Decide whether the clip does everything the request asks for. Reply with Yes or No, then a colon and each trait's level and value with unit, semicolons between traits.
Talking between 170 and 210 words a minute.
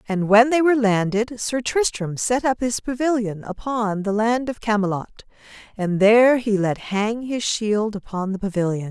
Yes: average, 175 wpm